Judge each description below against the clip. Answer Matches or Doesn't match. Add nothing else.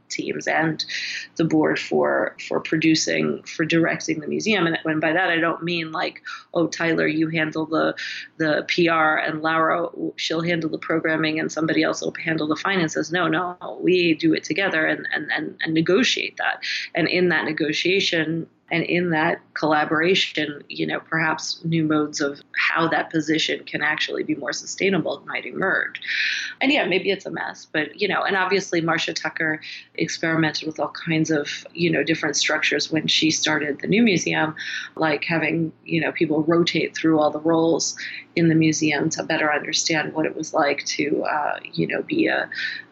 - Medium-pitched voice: Matches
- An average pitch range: Doesn't match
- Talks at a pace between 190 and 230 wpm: Doesn't match